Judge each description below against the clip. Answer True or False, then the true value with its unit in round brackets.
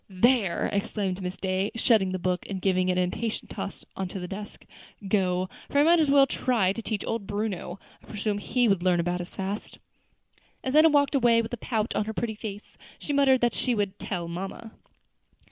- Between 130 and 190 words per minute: False (205 wpm)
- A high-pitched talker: True (205 Hz)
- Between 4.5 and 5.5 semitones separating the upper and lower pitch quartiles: False (4.0 semitones)